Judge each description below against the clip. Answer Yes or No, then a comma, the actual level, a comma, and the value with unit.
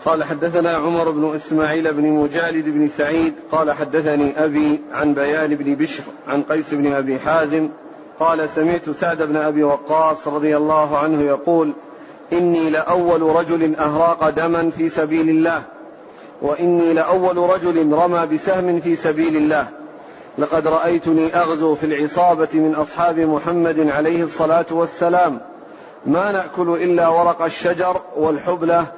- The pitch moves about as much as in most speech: No, narrow, 1.7 semitones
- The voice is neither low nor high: Yes, medium, 160 Hz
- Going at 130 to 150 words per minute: Yes, fast, 135 wpm